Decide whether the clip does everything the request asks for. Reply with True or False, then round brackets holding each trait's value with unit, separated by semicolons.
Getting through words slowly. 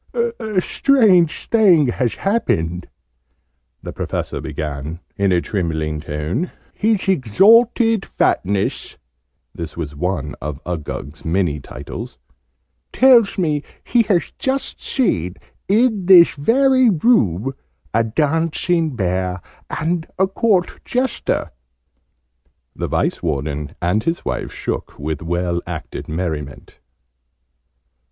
True (105 wpm)